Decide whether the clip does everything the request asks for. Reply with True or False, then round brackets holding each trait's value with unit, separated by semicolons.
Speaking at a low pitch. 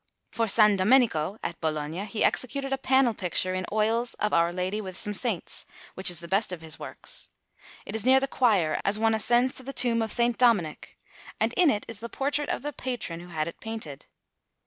False (215 Hz)